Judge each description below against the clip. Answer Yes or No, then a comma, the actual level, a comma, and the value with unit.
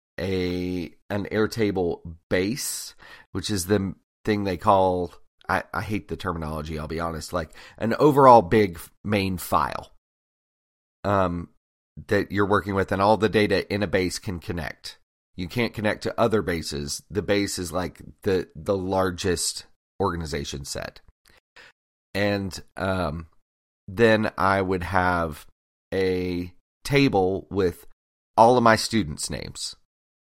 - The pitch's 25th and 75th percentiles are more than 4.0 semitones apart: No, average, 3.7 semitones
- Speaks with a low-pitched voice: Yes, very low, 90 Hz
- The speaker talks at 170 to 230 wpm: No, slow, 135 wpm